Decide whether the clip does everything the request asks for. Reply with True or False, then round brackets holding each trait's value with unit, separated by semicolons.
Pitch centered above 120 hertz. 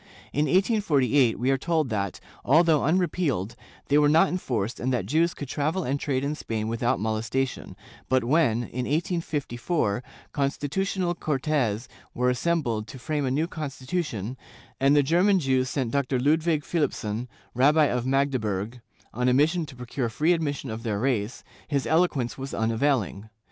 True (135 Hz)